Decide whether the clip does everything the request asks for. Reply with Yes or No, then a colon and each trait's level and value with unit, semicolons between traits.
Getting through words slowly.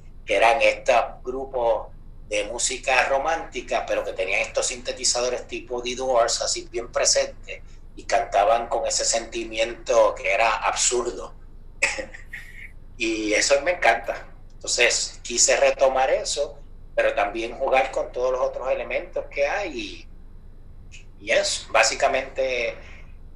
Yes: slow, 120 wpm